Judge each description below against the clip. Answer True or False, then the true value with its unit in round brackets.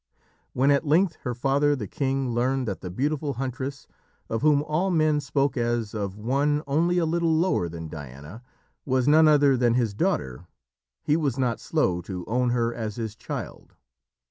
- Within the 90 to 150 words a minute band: False (175 wpm)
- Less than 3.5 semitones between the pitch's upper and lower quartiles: False (4.7 semitones)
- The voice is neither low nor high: False (130 Hz)